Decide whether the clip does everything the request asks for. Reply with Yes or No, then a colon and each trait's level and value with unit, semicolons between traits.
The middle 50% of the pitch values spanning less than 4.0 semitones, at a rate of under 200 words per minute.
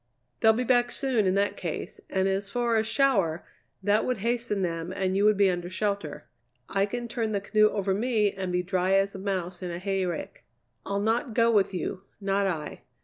No: average, 2.9 semitones; fast, 205 wpm